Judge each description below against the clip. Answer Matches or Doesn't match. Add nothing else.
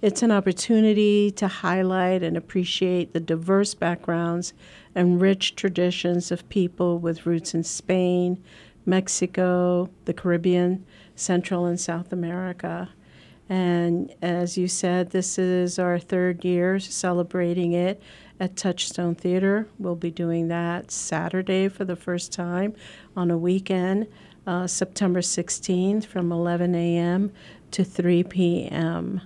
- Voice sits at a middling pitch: Matches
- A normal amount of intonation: Doesn't match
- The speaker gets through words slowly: Matches